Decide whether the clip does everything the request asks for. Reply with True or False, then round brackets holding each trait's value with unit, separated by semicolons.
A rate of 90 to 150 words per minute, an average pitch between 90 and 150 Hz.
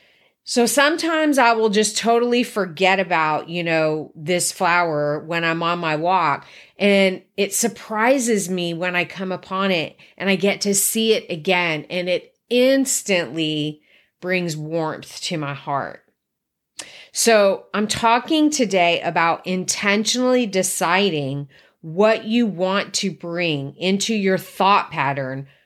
False (135 wpm; 185 Hz)